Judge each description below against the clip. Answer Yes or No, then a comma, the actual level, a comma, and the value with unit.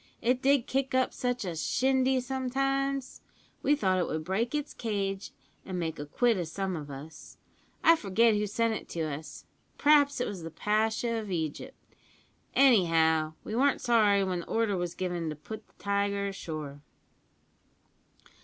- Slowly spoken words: No, average, 165 wpm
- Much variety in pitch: Yes, wide, 6.6 semitones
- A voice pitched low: No, high, 205 Hz